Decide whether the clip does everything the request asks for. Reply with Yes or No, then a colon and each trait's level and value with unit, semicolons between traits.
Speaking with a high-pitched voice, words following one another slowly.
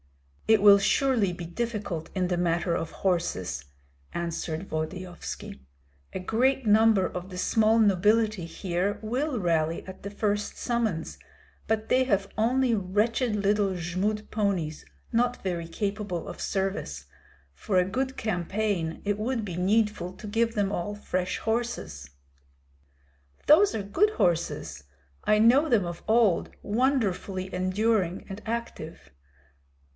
Yes: high, 200 Hz; slow, 130 wpm